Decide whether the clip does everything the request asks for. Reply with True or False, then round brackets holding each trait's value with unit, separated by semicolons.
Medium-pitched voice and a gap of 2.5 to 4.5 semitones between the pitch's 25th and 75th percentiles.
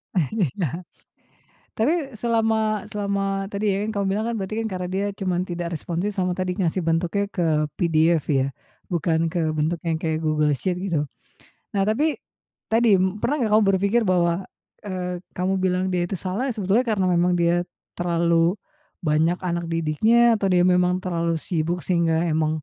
True (180 Hz; 2.9 semitones)